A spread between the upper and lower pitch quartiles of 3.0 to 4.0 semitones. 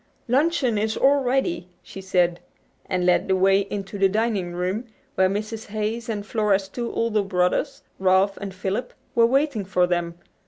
Yes: average, 3.7 semitones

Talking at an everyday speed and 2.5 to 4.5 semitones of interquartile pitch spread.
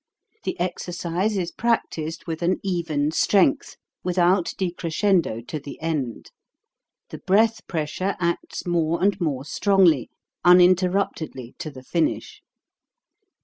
No: slow, 115 wpm; average, 3.2 semitones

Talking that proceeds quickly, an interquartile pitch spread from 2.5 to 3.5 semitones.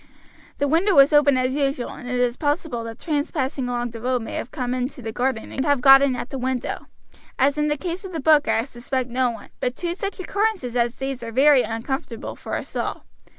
Yes: fast, 235 wpm; average, 3.2 semitones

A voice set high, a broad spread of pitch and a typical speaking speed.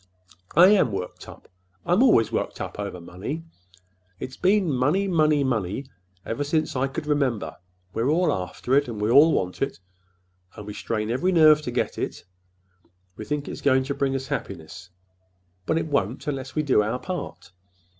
No: low, 135 Hz; wide, 6.0 semitones; average, 170 wpm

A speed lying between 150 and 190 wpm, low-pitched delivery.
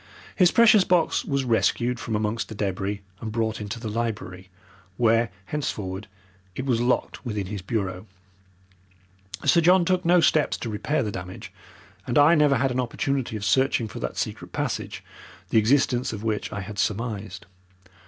Yes: average, 165 wpm; low, 115 Hz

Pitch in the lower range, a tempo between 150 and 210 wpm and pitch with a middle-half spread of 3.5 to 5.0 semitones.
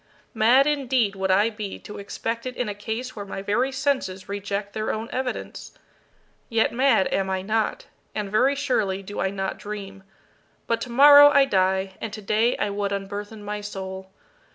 No: high, 210 Hz; average, 175 wpm; average, 3.8 semitones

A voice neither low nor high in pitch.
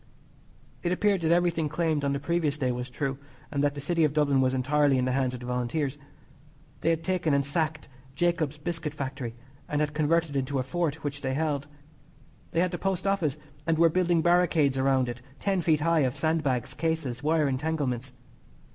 Yes: medium, 150 Hz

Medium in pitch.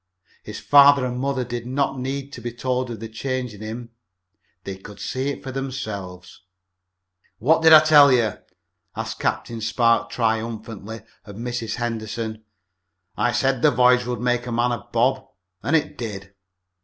No: low, 120 Hz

